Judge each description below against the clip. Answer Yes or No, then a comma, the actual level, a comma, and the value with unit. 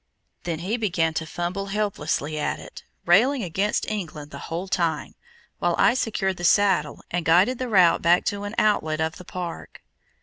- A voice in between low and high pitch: Yes, medium, 180 Hz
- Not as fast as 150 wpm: No, average, 175 wpm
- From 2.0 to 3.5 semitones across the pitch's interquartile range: No, average, 3.9 semitones